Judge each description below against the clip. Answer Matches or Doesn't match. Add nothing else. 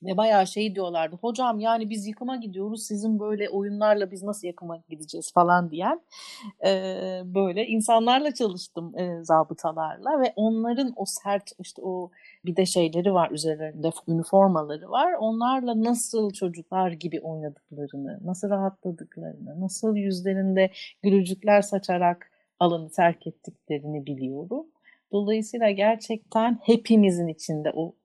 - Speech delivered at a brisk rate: Doesn't match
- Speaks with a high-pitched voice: Matches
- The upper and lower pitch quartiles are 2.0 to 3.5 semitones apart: Doesn't match